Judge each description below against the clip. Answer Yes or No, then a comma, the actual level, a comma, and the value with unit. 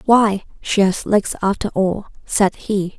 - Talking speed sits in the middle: Yes, average, 160 wpm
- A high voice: Yes, high, 200 Hz